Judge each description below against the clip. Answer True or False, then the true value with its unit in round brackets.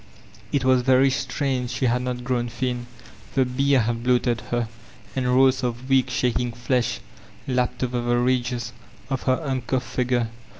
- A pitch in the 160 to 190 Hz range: False (125 Hz)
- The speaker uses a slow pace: False (160 wpm)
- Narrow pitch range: True (1.2 semitones)